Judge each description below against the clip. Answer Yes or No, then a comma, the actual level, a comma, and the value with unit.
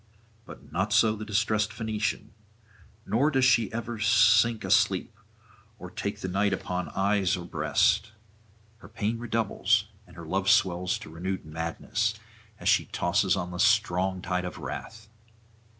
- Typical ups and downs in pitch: Yes, average, 3.2 semitones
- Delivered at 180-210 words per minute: No, average, 150 wpm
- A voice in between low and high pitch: No, low, 105 Hz